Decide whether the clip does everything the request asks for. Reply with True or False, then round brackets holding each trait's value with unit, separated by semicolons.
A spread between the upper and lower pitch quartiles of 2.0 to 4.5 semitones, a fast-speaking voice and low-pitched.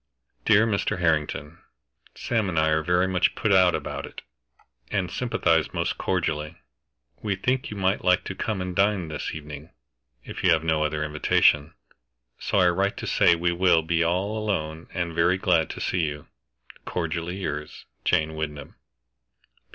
False (3.3 semitones; 165 wpm; 85 Hz)